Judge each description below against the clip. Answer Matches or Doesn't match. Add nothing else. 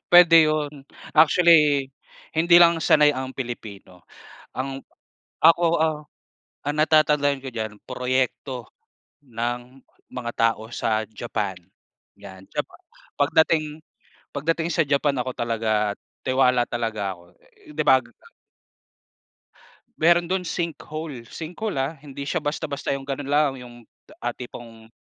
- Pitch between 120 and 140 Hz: Matches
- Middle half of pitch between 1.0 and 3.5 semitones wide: Doesn't match